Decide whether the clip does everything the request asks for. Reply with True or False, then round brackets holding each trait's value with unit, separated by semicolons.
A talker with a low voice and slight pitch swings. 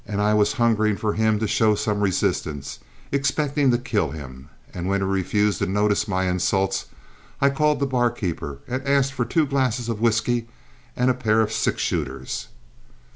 False (110 Hz; 4.4 semitones)